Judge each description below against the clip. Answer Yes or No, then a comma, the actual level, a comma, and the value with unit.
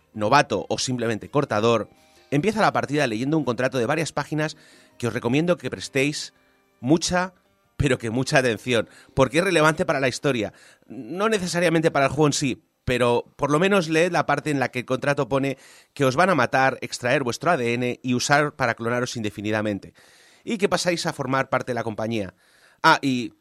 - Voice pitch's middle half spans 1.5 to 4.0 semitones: No, average, 4.6 semitones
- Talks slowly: No, average, 185 wpm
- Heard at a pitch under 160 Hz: Yes, low, 135 Hz